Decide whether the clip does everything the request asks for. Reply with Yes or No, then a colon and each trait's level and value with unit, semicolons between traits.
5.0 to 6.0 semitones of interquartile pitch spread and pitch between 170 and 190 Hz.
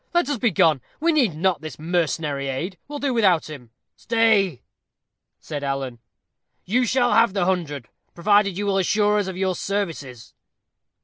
Yes: wide, 5.5 semitones; medium, 185 Hz